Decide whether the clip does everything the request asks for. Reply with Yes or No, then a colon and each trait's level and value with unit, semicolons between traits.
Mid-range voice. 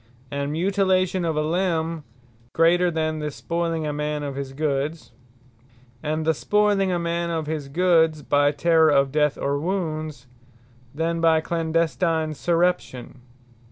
Yes: medium, 160 Hz